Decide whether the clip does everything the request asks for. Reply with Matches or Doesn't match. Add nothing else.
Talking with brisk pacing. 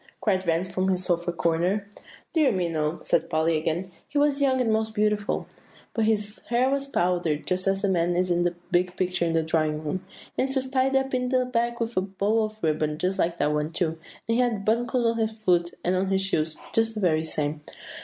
Matches